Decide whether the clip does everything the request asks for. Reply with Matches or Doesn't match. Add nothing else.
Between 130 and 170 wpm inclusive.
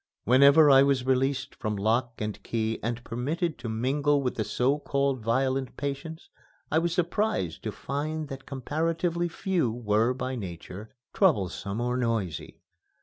Matches